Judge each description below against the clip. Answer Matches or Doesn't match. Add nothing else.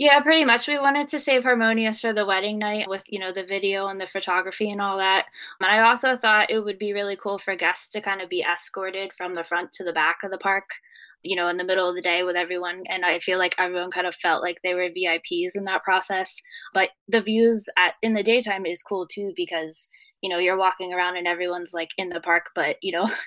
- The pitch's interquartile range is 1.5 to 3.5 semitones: Matches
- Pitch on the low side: Doesn't match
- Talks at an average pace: Doesn't match